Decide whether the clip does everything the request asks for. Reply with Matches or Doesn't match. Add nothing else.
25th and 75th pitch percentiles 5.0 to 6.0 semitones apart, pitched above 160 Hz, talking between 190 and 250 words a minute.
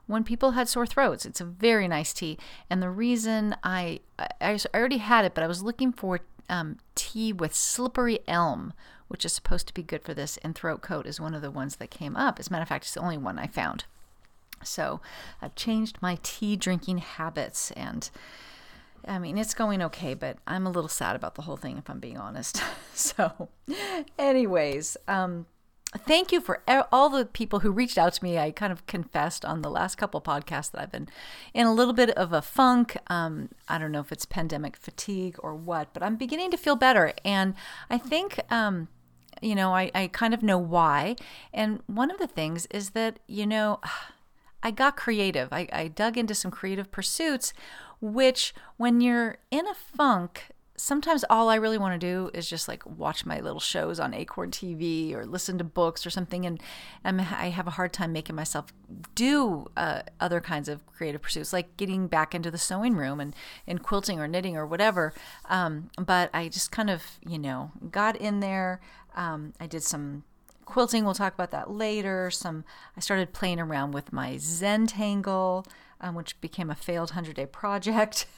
Matches